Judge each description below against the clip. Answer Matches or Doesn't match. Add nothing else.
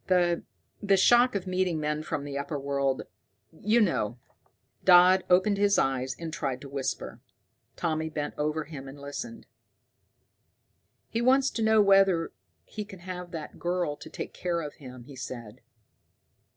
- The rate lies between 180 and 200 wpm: Doesn't match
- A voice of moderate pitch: Matches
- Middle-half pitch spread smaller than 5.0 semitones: Doesn't match